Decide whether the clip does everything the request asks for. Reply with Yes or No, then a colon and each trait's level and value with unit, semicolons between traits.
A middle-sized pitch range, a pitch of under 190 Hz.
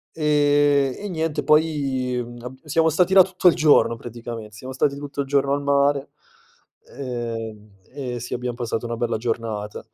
Yes: average, 3.6 semitones; low, 135 Hz